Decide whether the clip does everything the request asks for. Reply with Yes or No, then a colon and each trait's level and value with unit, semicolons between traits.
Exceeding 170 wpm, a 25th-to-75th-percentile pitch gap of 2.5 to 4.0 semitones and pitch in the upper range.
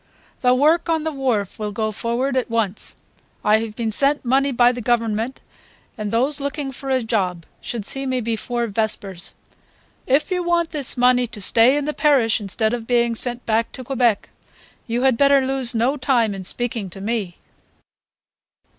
Yes: average, 180 wpm; average, 3.5 semitones; high, 240 Hz